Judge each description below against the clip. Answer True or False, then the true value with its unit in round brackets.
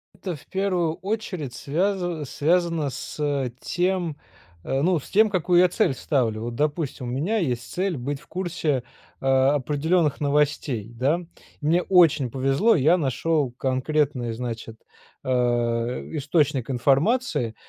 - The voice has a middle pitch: True (150 Hz)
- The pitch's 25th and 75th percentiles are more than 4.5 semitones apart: True (5.1 semitones)